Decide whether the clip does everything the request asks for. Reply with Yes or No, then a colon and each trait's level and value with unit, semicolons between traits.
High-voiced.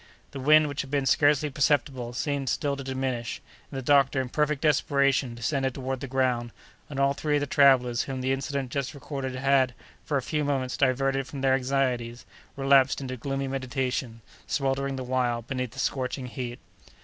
No: low, 135 Hz